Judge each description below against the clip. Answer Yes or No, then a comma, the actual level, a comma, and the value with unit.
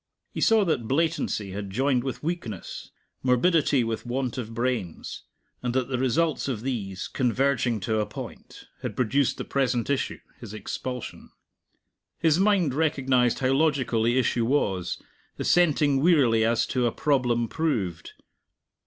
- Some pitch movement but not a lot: Yes, average, 3.7 semitones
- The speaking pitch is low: Yes, low, 125 Hz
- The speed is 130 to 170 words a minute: Yes, average, 145 wpm